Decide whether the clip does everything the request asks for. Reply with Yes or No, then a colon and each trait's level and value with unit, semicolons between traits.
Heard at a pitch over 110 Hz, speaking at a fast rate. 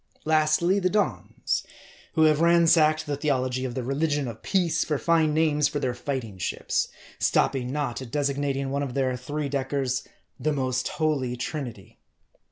No: medium, 140 Hz; average, 160 wpm